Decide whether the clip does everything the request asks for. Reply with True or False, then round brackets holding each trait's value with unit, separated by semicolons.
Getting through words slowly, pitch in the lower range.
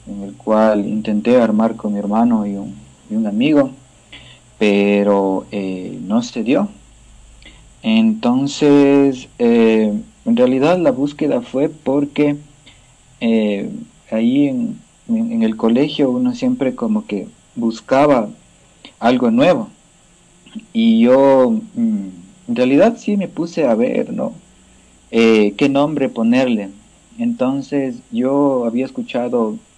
False (115 wpm; 145 Hz)